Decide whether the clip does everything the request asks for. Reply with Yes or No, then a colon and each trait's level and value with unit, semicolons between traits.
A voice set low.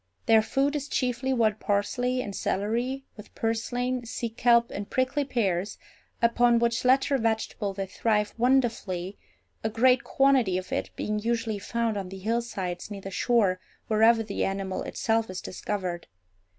No: high, 225 Hz